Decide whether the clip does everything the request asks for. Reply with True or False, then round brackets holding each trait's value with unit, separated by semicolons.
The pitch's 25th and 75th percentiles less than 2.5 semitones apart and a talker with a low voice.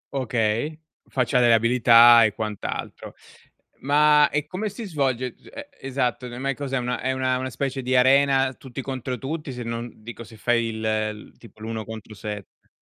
False (2.8 semitones; 125 Hz)